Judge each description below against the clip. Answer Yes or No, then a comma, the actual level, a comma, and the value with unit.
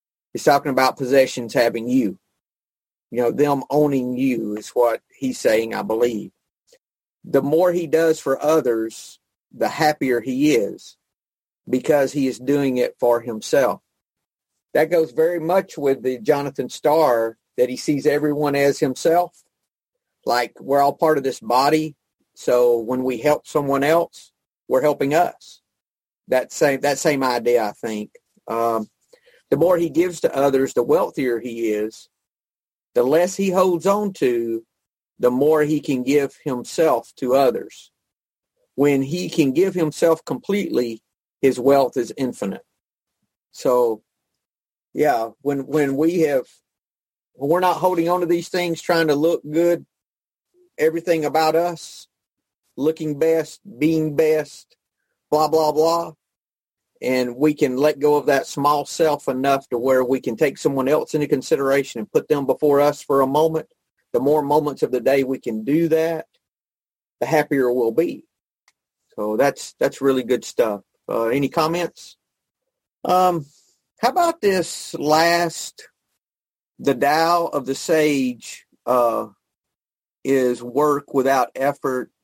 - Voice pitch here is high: No, medium, 145 Hz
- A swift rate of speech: No, average, 145 wpm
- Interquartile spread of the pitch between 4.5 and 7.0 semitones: No, average, 3.9 semitones